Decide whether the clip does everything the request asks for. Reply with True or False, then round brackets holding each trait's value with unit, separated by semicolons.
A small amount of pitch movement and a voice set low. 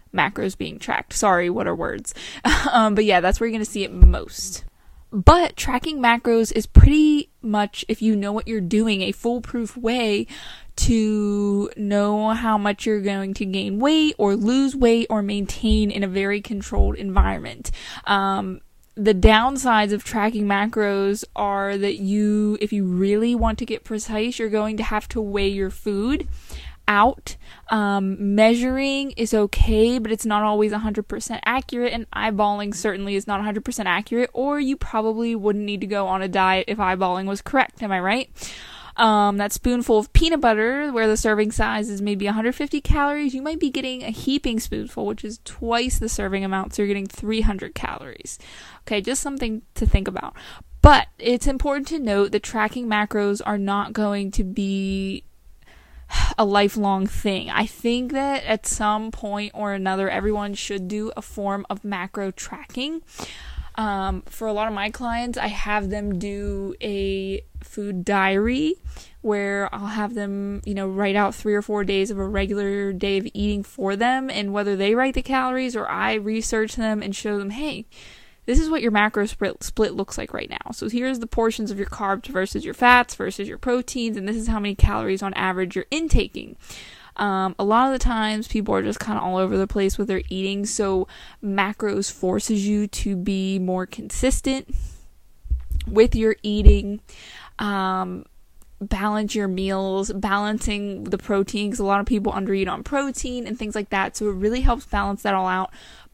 False (2.2 semitones; 210 Hz)